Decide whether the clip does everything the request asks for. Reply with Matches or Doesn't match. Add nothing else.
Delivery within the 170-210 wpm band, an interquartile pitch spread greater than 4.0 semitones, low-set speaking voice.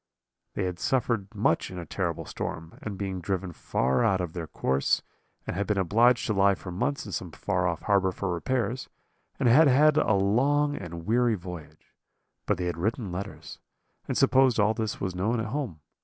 Matches